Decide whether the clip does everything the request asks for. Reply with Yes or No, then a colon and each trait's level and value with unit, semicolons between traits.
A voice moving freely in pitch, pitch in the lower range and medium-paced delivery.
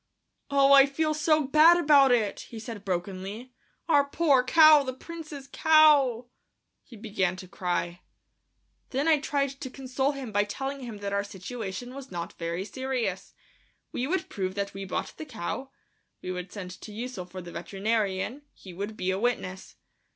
No: wide, 6.3 semitones; high, 240 Hz; average, 170 wpm